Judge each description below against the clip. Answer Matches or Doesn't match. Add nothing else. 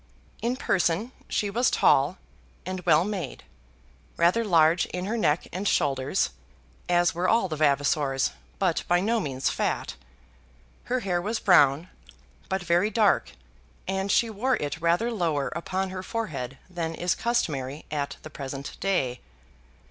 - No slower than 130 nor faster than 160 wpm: Matches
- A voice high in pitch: Doesn't match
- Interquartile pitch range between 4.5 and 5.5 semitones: Matches